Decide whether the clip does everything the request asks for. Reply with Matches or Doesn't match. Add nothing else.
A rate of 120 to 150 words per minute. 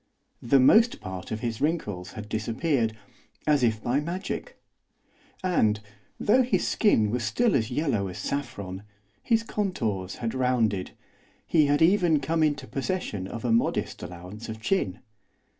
Matches